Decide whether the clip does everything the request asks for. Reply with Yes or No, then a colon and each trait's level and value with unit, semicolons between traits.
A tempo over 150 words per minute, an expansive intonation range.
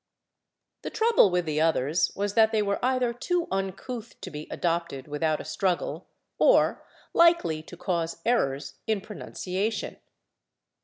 No: average, 140 wpm; wide, 6.0 semitones